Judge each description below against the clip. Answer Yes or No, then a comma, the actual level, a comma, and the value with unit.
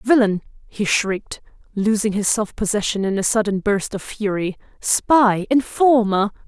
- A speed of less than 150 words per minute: Yes, average, 140 wpm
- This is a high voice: Yes, high, 210 Hz